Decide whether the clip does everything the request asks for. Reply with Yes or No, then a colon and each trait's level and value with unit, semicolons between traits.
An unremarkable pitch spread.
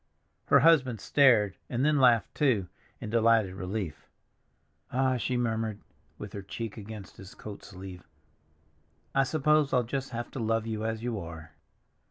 Yes: average, 3.9 semitones